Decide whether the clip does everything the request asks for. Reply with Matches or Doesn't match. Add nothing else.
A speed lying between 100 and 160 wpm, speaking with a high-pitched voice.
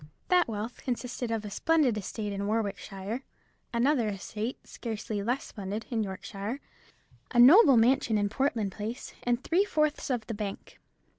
Matches